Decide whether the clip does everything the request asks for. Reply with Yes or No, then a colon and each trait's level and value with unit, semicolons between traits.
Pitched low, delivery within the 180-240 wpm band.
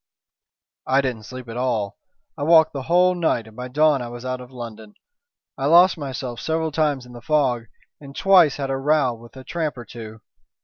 Yes: low, 130 Hz; fast, 205 wpm